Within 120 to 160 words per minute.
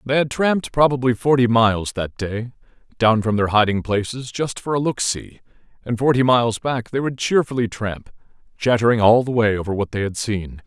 No: average, 195 wpm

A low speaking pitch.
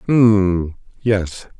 Yes: low, 100 Hz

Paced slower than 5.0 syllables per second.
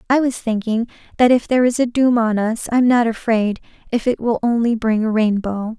No: 5.5 syllables/s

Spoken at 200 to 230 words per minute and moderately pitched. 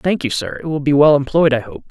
No: fast, 315 wpm; medium, 145 Hz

